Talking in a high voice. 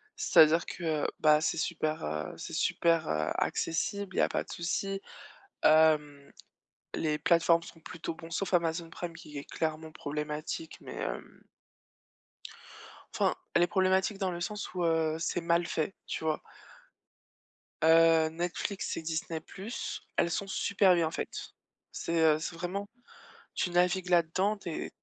No: medium, 165 Hz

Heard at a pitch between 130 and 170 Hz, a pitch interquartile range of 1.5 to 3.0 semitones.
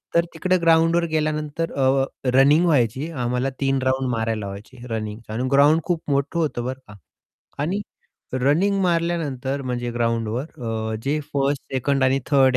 No: low, 135 Hz; average, 4.2 semitones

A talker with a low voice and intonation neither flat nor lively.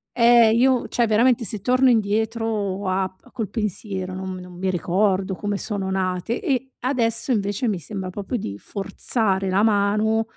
No: high, 205 Hz; average, 3.3 semitones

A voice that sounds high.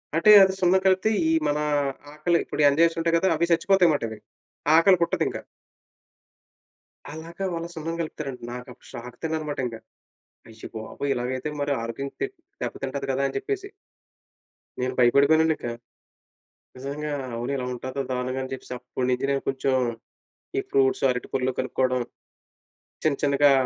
No: medium, 140 Hz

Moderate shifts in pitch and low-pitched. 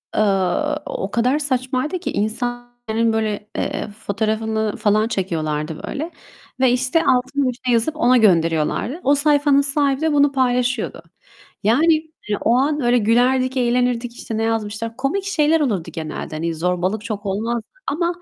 No: average, 4.4 semitones; high, 240 Hz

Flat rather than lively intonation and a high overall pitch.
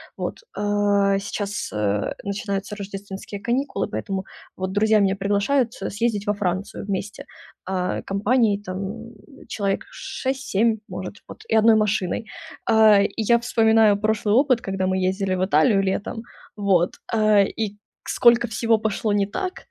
Yes: narrow, 2.2 semitones; high, 205 Hz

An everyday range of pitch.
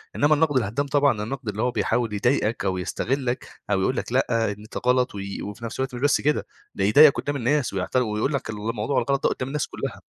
Yes: average, 4.5 semitones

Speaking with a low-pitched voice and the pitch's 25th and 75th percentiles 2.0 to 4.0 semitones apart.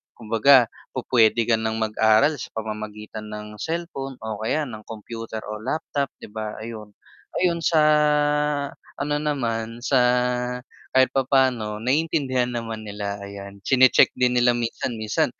Yes: low, 115 Hz; average, 3.6 semitones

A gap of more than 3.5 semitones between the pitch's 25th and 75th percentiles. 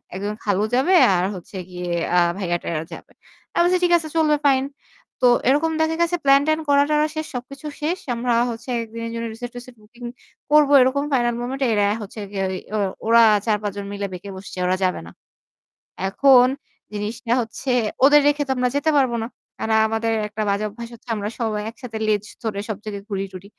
Yes: average, 5.1 semitones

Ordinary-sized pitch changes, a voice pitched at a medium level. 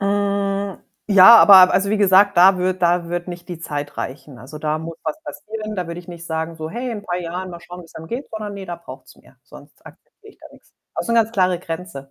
Yes: average, 3.3 semitones; medium, 180 Hz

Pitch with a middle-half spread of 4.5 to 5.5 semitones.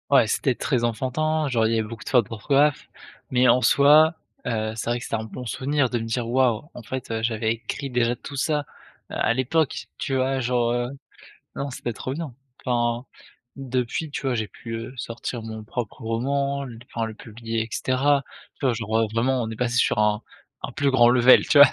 No: average, 2.8 semitones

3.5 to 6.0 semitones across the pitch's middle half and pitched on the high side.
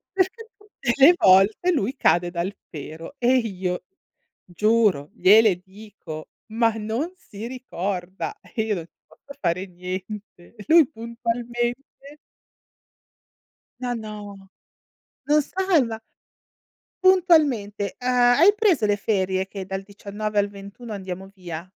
Yes: average, 4.7 semitones; high, 215 Hz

